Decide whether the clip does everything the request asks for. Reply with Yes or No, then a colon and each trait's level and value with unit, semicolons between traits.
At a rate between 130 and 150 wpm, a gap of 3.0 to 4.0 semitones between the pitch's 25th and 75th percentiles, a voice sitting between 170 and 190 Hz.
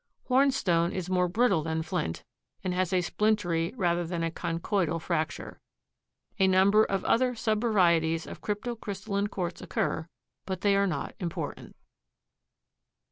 Yes: slow, 135 wpm; average, 3.6 semitones; medium, 185 Hz